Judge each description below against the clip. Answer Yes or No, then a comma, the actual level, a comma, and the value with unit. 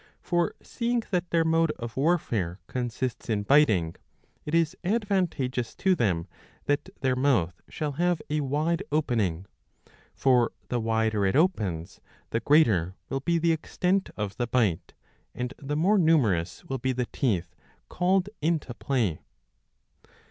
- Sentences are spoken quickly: No, average, 140 wpm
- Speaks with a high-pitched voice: No, low, 135 Hz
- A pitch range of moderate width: No, wide, 6.9 semitones